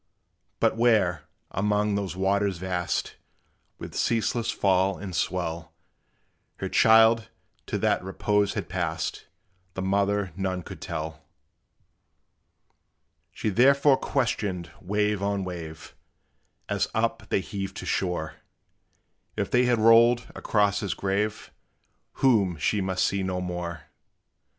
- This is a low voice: Yes, low, 100 Hz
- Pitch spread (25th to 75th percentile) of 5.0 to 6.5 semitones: No, average, 2.7 semitones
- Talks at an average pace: No, slow, 115 wpm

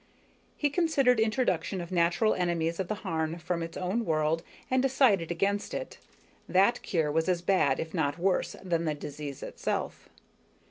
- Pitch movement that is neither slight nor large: Yes, average, 4.5 semitones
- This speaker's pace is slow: No, average, 165 wpm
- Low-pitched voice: No, medium, 175 Hz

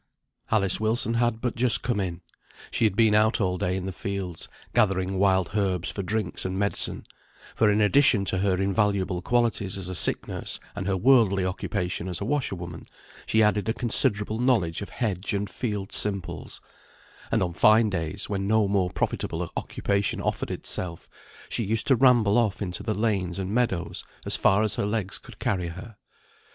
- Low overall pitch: Yes, low, 100 Hz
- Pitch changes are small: No, average, 3.0 semitones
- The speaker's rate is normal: Yes, average, 180 wpm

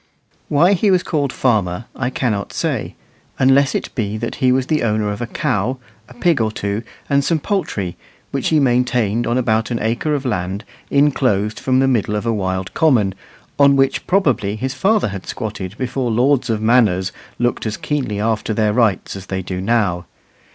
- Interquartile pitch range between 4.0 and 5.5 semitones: Yes, average, 4.5 semitones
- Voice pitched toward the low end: Yes, low, 120 Hz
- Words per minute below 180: No, average, 185 wpm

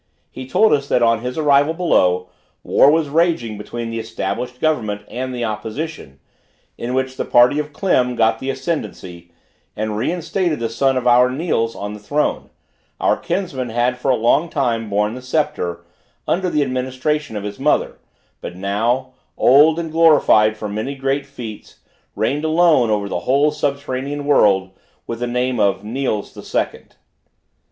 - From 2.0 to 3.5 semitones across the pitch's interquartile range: No, average, 4.9 semitones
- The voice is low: Yes, low, 125 Hz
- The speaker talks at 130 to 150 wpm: No, average, 165 wpm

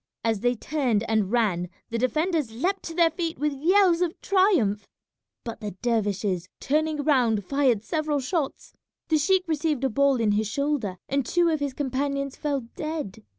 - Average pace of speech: Yes, average, 170 wpm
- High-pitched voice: Yes, very high, 275 Hz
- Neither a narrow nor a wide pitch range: No, wide, 5.8 semitones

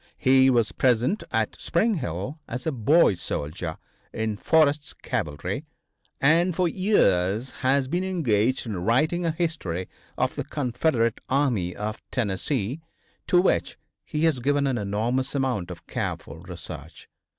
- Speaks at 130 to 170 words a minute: Yes, average, 140 wpm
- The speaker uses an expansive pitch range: Yes, wide, 7.0 semitones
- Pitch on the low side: Yes, low, 130 Hz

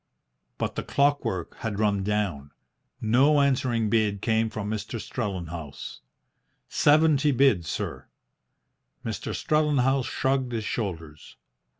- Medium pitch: No, low, 110 Hz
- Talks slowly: Yes, slow, 105 wpm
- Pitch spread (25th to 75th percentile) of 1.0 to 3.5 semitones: No, average, 5.1 semitones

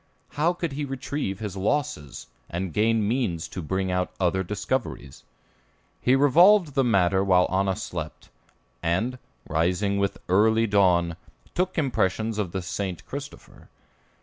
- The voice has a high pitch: No, low, 100 Hz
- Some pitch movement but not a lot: No, wide, 6.1 semitones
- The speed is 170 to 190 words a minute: No, slow, 135 wpm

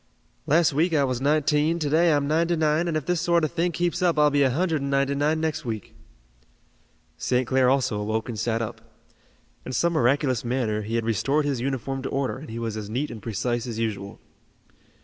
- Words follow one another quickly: Yes, fast, 215 wpm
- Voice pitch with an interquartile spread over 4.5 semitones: Yes, average, 4.9 semitones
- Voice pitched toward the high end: No, low, 135 Hz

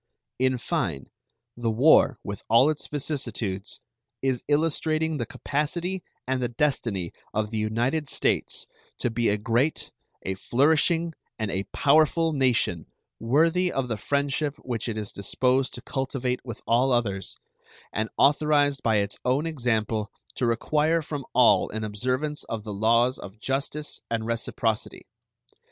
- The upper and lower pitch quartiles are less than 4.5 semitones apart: No, average, 4.9 semitones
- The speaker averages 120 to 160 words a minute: Yes, average, 140 wpm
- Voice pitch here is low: Yes, low, 125 Hz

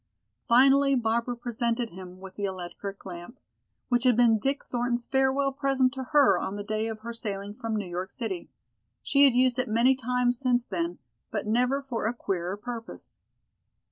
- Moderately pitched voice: No, high, 235 Hz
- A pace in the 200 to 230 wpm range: No, average, 175 wpm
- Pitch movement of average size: Yes, average, 3.9 semitones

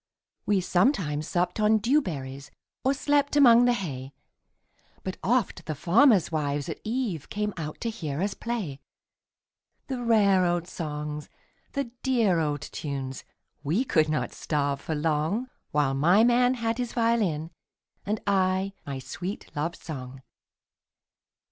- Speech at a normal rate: No, slow, 120 wpm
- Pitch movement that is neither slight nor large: No, wide, 7.5 semitones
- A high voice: No, medium, 180 Hz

